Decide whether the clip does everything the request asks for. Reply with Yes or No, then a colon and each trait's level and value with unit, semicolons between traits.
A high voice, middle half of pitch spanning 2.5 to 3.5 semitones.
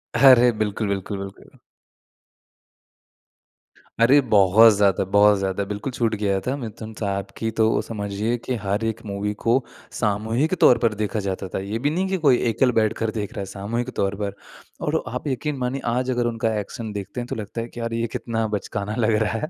No: low, 110 Hz; average, 2.9 semitones